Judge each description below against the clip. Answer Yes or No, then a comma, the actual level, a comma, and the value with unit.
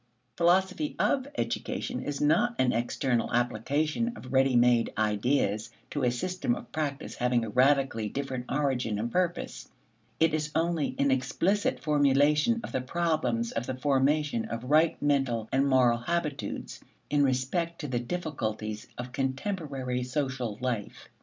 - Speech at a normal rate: Yes, average, 145 wpm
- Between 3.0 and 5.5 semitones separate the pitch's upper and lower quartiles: Yes, average, 3.9 semitones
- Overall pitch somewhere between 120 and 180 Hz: Yes, low, 135 Hz